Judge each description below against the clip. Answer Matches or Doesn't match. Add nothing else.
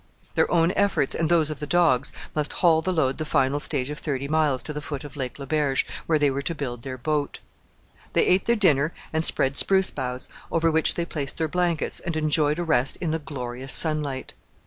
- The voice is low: Doesn't match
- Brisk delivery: Matches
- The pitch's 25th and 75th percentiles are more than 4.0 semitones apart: Doesn't match